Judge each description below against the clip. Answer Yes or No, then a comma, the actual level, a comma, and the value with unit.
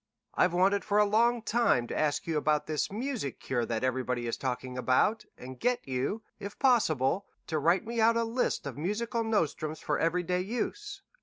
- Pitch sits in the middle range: Yes, medium, 180 Hz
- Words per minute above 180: Yes, average, 190 wpm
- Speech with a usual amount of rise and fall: No, wide, 8.7 semitones